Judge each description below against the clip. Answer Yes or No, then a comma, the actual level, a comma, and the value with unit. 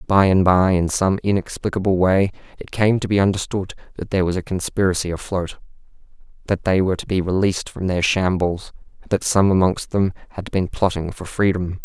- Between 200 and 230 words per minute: No, average, 180 wpm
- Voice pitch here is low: Yes, very low, 95 Hz